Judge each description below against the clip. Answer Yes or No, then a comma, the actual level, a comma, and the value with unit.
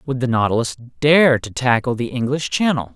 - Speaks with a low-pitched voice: Yes, low, 130 Hz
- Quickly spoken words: No, average, 185 wpm